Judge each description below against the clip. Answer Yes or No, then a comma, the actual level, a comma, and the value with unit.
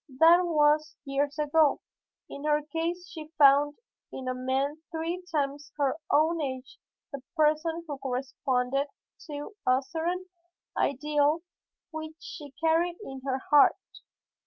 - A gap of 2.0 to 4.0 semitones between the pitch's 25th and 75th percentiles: Yes, average, 2.8 semitones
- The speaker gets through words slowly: Yes, slow, 130 wpm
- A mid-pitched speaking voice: No, very high, 295 Hz